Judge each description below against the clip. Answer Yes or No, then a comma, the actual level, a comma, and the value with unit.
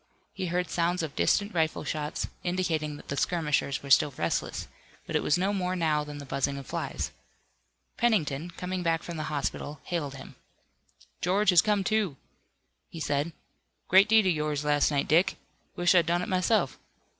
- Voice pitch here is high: No, medium, 165 Hz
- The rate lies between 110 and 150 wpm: No, average, 180 wpm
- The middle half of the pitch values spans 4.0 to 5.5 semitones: No, average, 3.6 semitones